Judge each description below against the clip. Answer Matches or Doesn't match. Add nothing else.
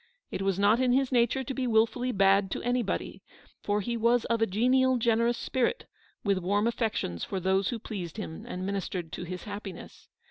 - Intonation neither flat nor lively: Matches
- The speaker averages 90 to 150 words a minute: Doesn't match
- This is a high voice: Matches